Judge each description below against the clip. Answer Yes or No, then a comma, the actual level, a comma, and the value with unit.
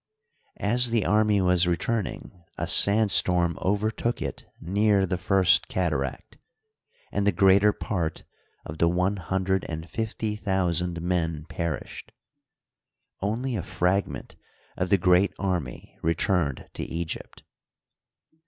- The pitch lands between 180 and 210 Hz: No, very low, 95 Hz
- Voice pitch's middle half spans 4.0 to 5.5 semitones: No, average, 3.0 semitones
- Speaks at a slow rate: Yes, slow, 125 wpm